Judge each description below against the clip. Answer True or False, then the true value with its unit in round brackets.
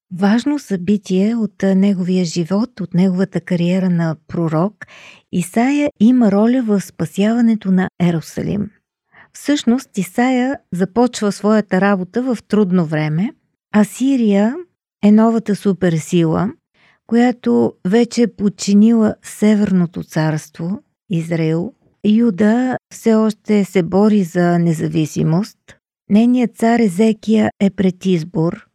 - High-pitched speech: True (205 Hz)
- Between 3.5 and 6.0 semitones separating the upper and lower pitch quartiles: True (3.8 semitones)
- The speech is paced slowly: True (105 wpm)